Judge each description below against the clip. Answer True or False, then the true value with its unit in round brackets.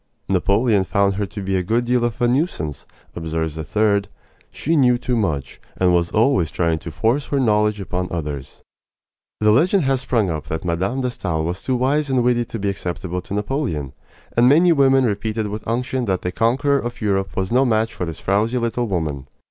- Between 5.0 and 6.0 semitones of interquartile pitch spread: True (5.5 semitones)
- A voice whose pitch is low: True (105 Hz)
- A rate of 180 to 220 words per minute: True (205 wpm)